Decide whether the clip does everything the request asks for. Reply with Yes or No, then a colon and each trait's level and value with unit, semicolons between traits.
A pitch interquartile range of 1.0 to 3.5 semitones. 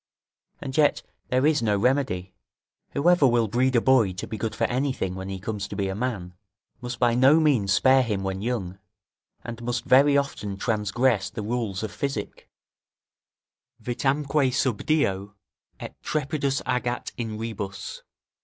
No: average, 4.6 semitones